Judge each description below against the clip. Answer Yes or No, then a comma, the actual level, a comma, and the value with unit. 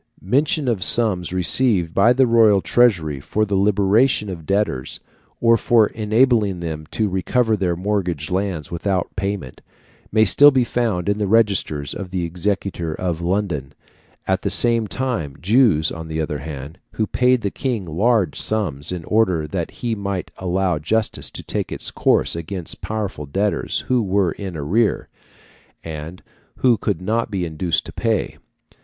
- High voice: No, very low, 95 Hz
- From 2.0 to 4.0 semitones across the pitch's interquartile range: No, average, 4.7 semitones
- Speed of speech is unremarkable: Yes, average, 160 wpm